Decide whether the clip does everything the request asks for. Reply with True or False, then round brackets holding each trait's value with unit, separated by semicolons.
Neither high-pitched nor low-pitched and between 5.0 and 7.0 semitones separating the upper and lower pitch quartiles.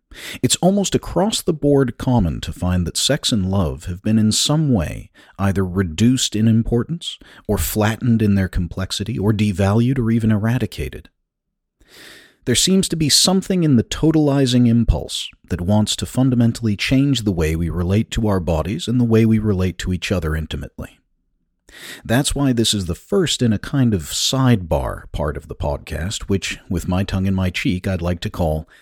False (105 Hz; 5.3 semitones)